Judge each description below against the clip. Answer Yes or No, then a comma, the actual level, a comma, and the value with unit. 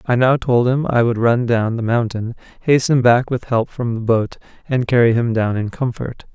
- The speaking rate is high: Yes, fast, 220 wpm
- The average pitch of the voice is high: No, low, 120 Hz